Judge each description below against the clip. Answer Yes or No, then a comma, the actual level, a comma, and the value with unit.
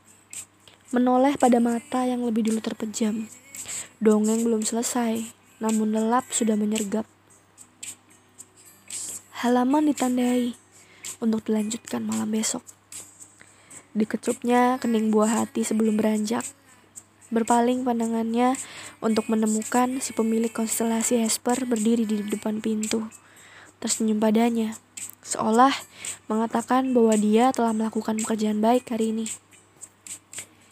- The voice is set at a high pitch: Yes, high, 225 Hz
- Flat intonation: Yes, narrow, 1.8 semitones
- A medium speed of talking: No, slow, 100 wpm